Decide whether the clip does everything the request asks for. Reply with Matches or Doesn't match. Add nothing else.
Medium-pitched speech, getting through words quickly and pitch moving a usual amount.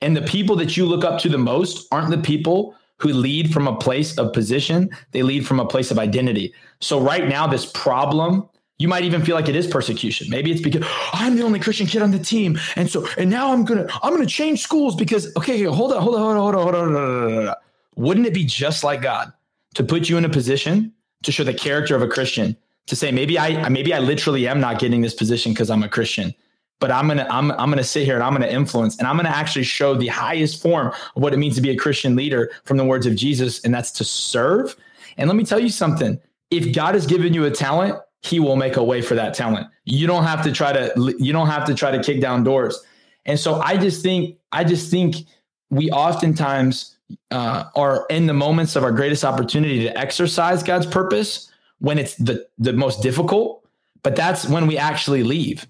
Matches